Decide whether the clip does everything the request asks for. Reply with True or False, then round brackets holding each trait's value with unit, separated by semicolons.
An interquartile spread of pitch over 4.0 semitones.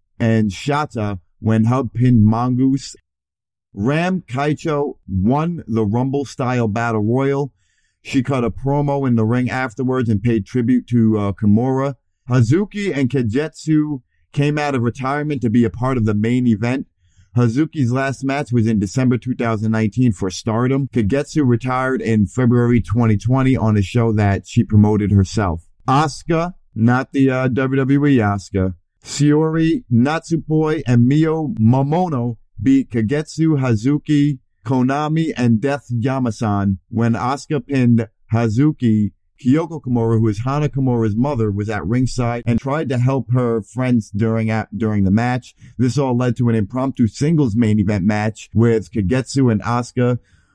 False (3.6 semitones)